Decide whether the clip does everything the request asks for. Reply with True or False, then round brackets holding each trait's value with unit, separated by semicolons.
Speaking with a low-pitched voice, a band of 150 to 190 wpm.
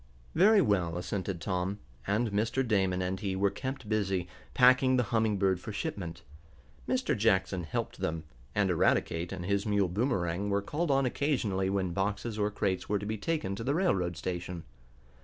True (100 Hz; 175 wpm)